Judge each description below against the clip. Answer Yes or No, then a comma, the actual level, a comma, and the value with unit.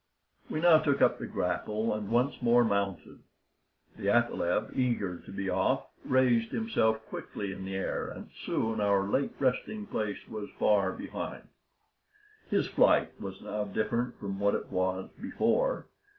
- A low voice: Yes, low, 110 Hz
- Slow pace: No, average, 150 wpm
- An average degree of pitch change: Yes, average, 3.7 semitones